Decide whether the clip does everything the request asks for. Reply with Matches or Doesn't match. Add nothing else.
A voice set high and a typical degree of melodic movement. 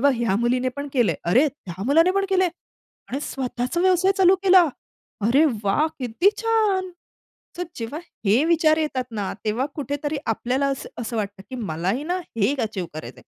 Doesn't match